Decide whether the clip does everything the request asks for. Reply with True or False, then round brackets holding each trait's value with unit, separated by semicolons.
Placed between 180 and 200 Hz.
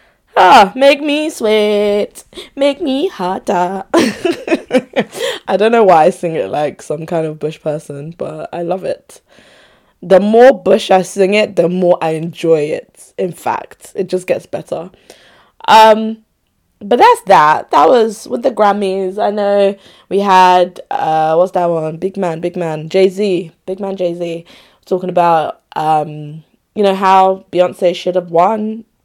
True (190 Hz)